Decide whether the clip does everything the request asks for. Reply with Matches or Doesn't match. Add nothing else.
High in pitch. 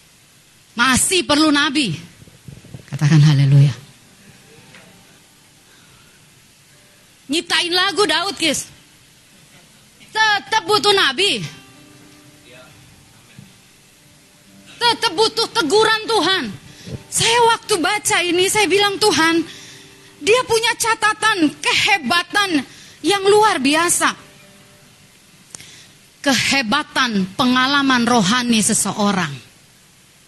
Matches